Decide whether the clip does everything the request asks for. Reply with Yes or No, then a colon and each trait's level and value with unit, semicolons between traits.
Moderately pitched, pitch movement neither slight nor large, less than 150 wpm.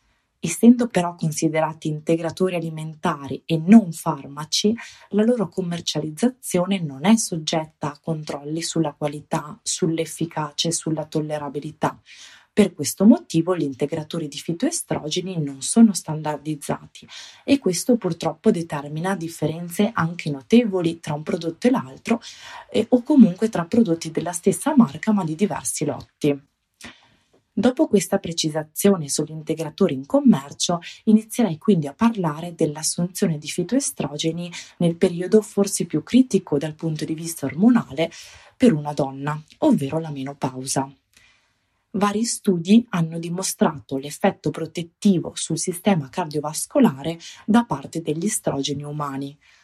Yes: medium, 165 Hz; average, 4.8 semitones; average, 120 wpm